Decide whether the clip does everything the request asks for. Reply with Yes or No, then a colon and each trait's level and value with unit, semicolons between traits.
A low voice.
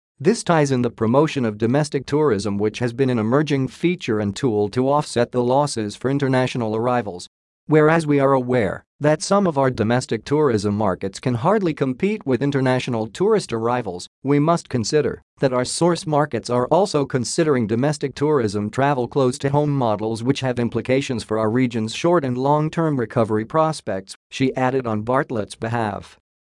Yes: low, 130 Hz